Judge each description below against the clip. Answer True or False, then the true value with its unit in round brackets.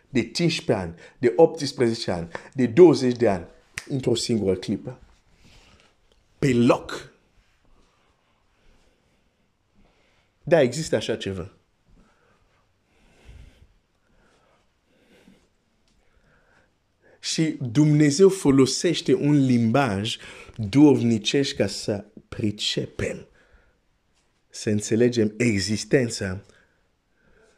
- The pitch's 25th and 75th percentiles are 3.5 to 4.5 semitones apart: False (5.0 semitones)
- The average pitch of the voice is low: True (120 Hz)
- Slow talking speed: True (70 wpm)